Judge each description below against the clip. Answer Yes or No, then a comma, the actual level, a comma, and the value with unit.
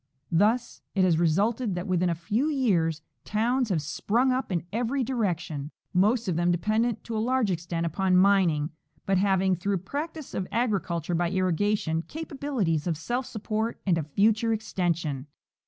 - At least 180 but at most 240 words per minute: No, average, 165 wpm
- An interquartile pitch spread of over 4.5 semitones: Yes, average, 5.1 semitones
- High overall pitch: Yes, high, 195 Hz